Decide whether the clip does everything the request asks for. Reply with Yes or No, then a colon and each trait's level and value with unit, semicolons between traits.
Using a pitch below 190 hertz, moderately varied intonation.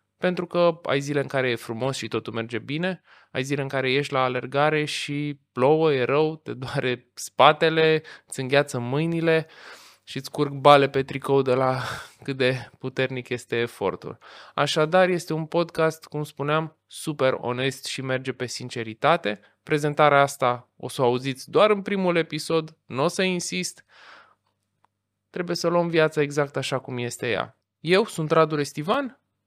Yes: medium, 140 Hz; average, 3.6 semitones